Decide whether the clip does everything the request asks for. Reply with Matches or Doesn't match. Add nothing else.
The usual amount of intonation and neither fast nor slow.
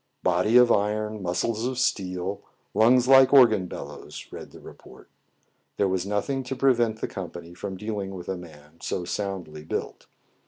Matches